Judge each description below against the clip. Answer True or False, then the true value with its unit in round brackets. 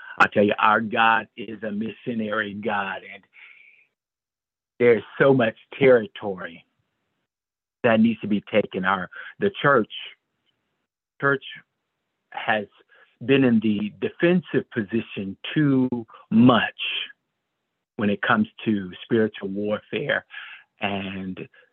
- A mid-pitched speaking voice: False (110 Hz)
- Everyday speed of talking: False (105 wpm)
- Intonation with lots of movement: False (3.5 semitones)